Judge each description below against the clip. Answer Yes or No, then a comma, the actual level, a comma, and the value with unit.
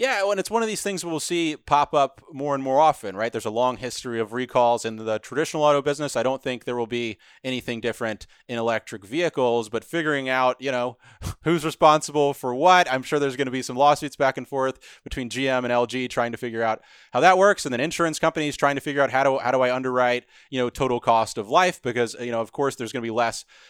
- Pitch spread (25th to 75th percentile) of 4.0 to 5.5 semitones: No, average, 3.5 semitones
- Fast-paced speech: Yes, fast, 250 wpm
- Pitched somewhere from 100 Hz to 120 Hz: No, low, 130 Hz